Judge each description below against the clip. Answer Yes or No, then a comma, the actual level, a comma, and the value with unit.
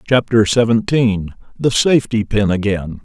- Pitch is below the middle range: Yes, low, 110 Hz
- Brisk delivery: No, slow, 120 wpm